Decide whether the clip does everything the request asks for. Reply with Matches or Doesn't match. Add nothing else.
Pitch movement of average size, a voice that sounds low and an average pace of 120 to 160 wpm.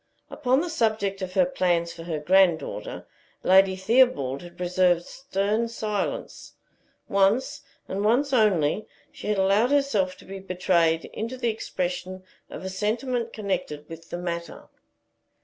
Doesn't match